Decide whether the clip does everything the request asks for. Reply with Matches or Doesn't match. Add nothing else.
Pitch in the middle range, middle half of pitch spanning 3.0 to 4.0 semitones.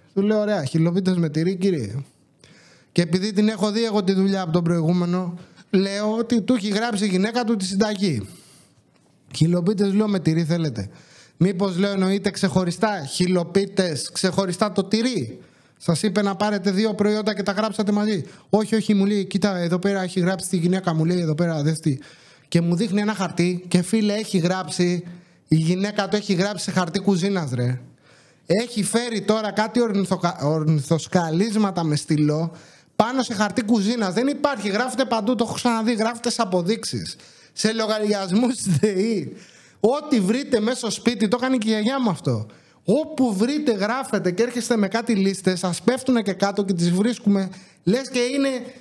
Doesn't match